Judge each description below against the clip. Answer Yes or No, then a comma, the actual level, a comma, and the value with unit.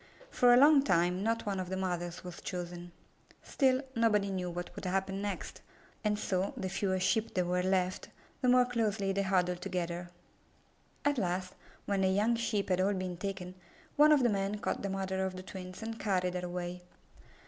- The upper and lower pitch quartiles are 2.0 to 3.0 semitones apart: Yes, narrow, 2.6 semitones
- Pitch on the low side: No, high, 190 Hz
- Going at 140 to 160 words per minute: No, average, 190 wpm